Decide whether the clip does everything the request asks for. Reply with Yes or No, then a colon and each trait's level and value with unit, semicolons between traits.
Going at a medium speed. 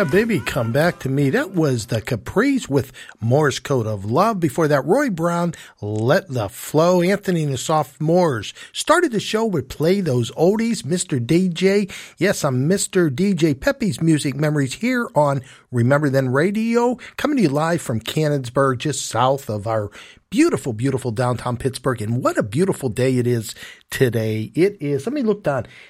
Yes: average, 175 wpm